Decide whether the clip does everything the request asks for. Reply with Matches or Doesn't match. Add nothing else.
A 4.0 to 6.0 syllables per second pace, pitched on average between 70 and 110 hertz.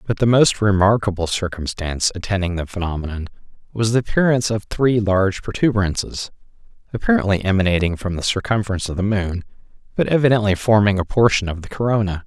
Doesn't match